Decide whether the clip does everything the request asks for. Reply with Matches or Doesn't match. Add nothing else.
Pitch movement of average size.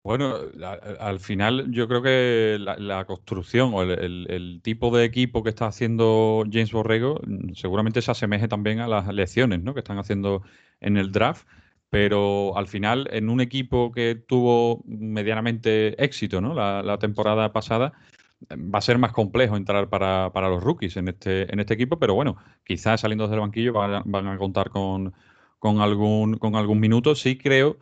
Matches